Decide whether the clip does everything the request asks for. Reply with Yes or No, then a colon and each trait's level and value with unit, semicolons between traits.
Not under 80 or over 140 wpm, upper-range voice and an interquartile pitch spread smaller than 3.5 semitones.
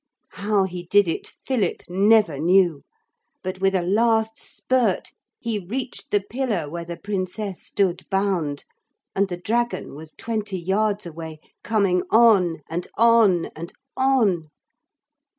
No: slow, 135 wpm; high, 195 Hz; average, 3.9 semitones